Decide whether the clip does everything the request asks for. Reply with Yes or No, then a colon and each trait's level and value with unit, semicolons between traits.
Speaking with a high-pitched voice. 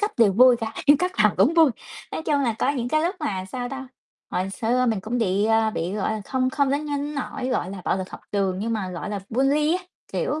Yes: high, 245 Hz